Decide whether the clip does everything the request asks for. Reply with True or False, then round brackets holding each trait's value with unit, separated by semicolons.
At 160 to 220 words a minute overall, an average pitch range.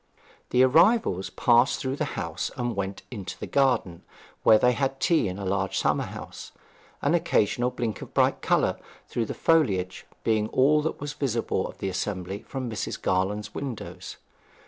False (170 wpm; 5.7 semitones)